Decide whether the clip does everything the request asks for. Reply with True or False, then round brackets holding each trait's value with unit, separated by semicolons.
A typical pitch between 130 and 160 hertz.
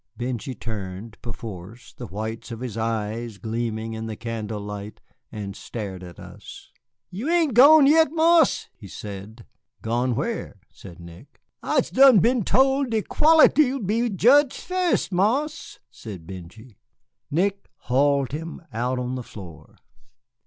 False (120 Hz)